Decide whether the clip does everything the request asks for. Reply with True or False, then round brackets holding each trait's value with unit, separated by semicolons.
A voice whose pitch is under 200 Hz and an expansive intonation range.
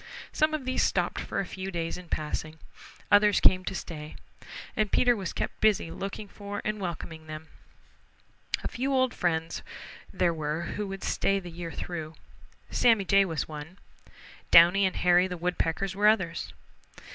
False (185 Hz; 3.7 semitones)